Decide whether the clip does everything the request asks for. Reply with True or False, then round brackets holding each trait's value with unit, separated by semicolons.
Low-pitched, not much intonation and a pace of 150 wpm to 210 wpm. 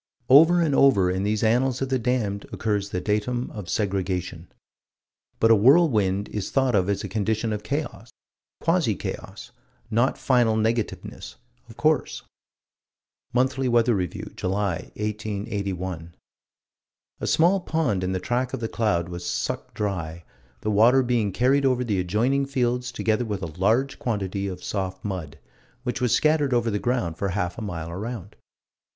False (110 Hz; 4.6 semitones; 155 wpm)